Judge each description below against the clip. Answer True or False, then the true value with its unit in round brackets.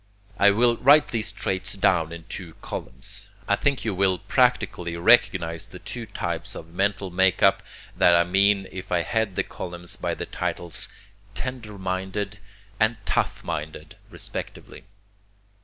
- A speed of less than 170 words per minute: True (150 wpm)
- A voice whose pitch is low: True (95 Hz)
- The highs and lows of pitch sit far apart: False (3.3 semitones)